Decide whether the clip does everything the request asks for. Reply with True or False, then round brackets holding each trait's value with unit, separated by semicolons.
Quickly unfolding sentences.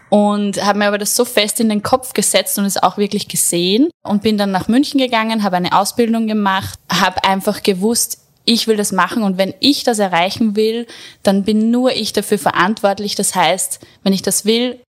True (205 wpm)